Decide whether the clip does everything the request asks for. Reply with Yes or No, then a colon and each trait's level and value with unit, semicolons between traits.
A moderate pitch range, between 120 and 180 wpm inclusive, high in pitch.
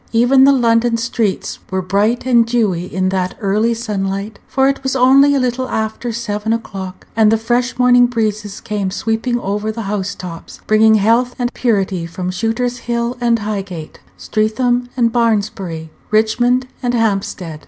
Yes: average, 3.4 semitones; average, 160 wpm; high, 225 Hz